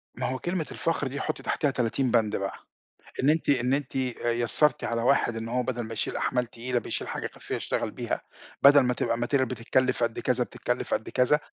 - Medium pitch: No, low, 125 Hz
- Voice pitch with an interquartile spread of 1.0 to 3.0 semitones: Yes, average, 2.7 semitones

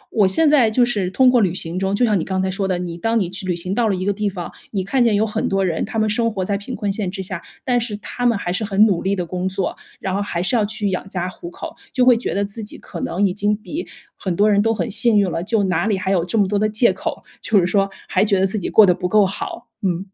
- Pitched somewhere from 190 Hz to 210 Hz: Yes, high, 200 Hz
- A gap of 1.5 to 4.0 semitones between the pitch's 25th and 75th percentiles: Yes, average, 2.7 semitones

